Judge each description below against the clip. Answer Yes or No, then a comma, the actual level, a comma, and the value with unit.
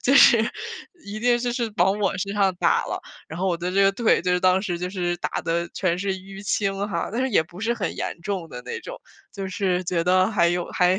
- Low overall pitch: No, high, 190 Hz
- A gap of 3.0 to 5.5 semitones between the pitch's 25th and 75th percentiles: No, narrow, 2.4 semitones